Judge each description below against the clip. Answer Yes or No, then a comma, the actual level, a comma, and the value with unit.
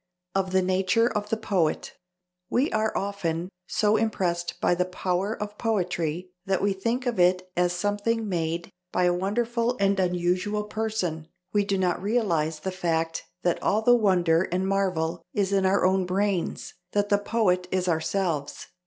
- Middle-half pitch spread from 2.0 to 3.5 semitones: Yes, average, 2.8 semitones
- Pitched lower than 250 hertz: Yes, high, 190 Hz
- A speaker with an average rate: Yes, average, 165 wpm